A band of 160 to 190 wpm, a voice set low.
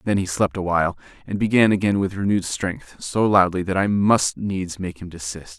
No: fast, 205 wpm; very low, 95 Hz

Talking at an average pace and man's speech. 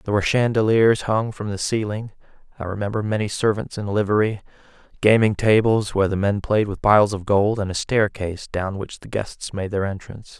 Yes: average, 190 wpm; male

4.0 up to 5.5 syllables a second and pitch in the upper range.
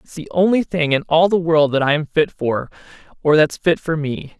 No: 5.0 syllables/s; medium, 160 Hz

